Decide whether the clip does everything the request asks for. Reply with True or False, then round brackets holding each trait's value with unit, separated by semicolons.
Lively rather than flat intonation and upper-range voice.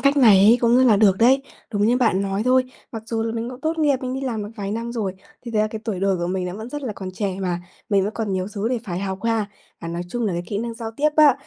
False (3.9 semitones; 220 Hz)